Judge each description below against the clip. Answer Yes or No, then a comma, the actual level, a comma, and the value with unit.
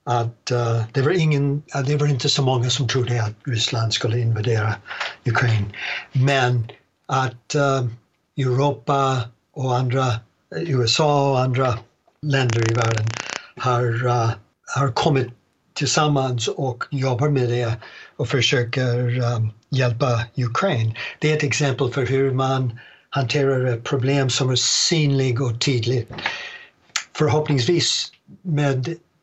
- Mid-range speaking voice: No, low, 130 Hz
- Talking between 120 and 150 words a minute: Yes, slow, 125 wpm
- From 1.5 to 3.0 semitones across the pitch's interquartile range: Yes, narrow, 2.6 semitones